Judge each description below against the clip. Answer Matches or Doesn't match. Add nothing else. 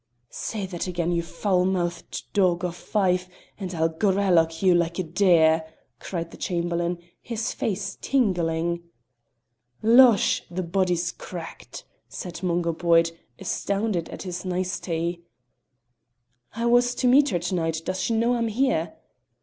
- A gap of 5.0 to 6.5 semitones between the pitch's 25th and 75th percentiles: Doesn't match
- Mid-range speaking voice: Matches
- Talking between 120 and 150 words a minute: Matches